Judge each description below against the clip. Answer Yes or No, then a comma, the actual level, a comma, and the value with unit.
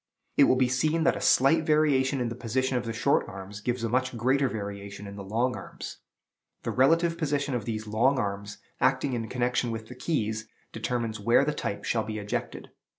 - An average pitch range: Yes, average, 3.5 semitones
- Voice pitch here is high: No, low, 120 Hz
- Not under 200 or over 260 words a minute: Yes, fast, 205 wpm